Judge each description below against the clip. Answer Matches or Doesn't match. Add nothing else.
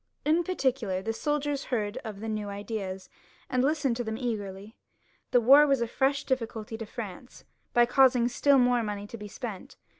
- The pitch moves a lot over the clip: Doesn't match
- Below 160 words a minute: Doesn't match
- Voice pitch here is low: Doesn't match